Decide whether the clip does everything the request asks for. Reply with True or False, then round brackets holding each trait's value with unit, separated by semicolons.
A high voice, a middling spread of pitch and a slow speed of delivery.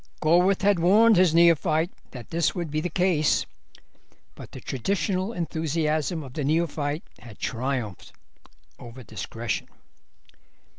False (160 Hz; 4.3 semitones; 120 wpm)